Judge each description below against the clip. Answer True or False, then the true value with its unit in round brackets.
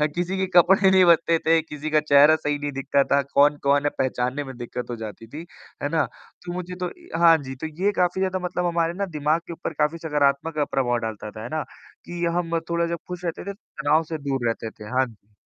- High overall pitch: False (155 Hz)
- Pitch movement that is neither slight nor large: True (3.9 semitones)